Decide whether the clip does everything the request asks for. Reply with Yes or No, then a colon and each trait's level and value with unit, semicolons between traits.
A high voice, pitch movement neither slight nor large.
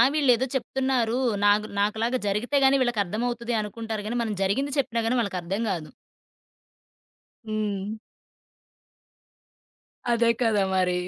Yes: high, 225 Hz; average, 3.0 semitones